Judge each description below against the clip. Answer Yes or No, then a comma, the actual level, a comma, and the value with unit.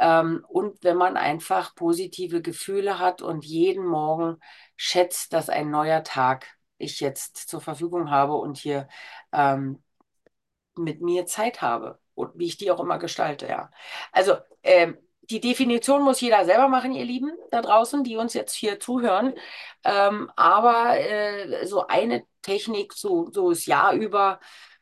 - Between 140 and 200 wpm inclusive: Yes, average, 150 wpm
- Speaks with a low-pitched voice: No, high, 200 Hz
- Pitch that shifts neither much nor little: No, wide, 7.5 semitones